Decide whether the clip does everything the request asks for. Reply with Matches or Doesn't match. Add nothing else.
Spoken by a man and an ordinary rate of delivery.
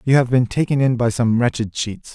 Doesn't match